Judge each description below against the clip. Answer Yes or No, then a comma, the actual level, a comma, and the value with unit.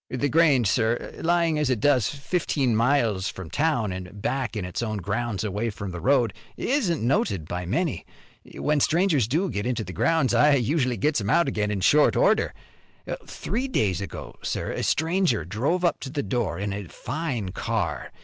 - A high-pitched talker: No, low, 120 Hz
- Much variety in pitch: Yes, wide, 6.8 semitones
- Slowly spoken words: No, average, 185 wpm